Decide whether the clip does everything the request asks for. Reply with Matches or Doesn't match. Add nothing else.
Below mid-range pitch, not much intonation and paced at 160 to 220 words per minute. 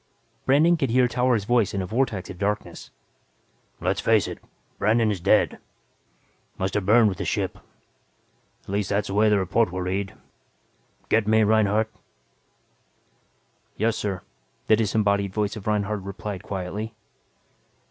Doesn't match